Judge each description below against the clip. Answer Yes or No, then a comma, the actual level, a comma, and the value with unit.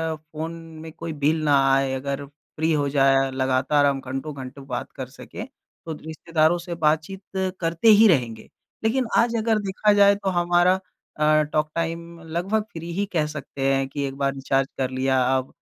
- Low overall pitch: No, medium, 155 Hz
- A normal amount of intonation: Yes, average, 4.0 semitones